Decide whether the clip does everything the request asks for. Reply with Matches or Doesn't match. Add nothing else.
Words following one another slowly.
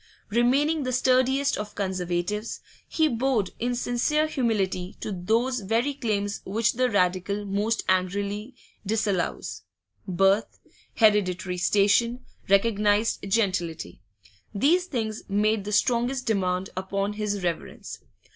Matches